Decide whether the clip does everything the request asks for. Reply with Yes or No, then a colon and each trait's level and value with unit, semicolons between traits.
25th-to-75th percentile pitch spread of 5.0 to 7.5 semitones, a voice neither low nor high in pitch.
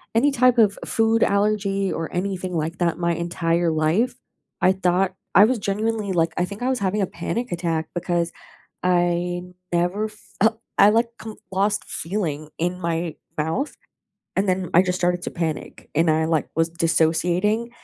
No: average, 3.7 semitones; medium, 180 Hz